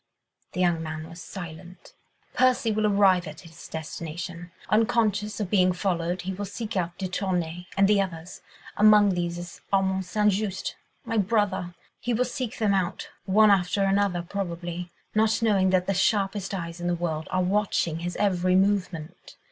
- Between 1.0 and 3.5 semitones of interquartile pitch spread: Yes, average, 2.8 semitones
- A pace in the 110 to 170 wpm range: Yes, average, 165 wpm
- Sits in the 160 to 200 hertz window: Yes, medium, 185 Hz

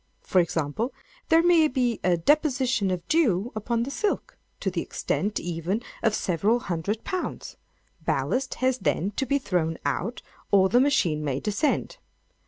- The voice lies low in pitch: No, high, 220 Hz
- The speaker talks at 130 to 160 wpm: Yes, average, 155 wpm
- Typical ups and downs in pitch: No, wide, 6.7 semitones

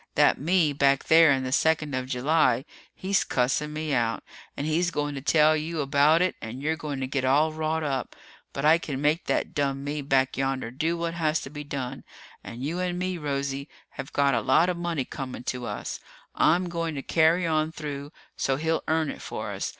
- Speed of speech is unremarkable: No, fast, 210 wpm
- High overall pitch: No, medium, 150 Hz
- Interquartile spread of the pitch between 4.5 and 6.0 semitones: No, average, 3.0 semitones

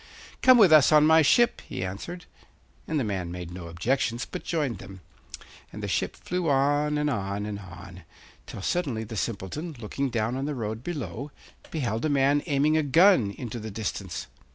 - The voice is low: Yes, low, 130 Hz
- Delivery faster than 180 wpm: Yes, average, 190 wpm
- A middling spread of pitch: No, wide, 7.0 semitones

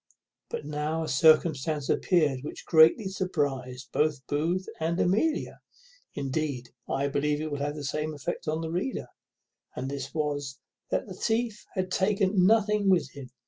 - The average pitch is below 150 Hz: No, medium, 155 Hz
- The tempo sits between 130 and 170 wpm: Yes, average, 155 wpm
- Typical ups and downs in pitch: Yes, average, 4.4 semitones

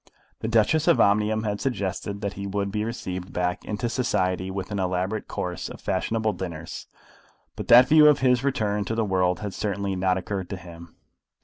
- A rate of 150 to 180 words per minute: No, average, 190 wpm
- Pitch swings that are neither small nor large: Yes, average, 3.2 semitones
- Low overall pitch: Yes, low, 100 Hz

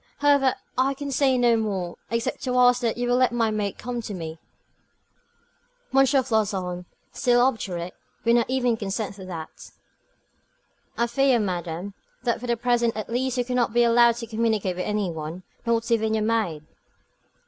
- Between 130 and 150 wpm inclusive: No, average, 175 wpm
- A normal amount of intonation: Yes, average, 3.7 semitones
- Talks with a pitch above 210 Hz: Yes, high, 230 Hz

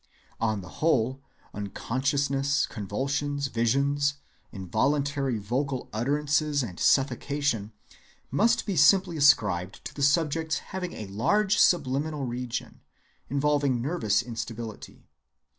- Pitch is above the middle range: No, medium, 140 Hz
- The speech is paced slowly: Yes, slow, 100 wpm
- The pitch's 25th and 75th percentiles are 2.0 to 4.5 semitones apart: Yes, average, 4.0 semitones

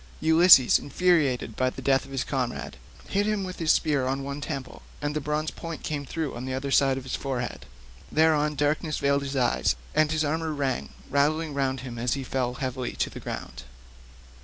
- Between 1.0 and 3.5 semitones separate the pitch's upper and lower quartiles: Yes, average, 2.8 semitones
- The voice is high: No, medium, 140 Hz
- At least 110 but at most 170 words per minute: No, average, 200 wpm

